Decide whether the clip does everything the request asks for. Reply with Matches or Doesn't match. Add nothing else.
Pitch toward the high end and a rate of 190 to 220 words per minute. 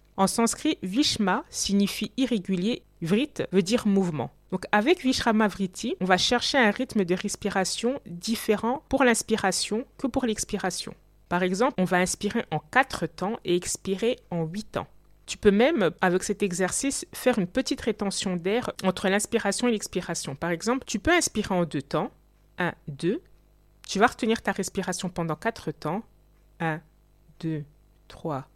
Doesn't match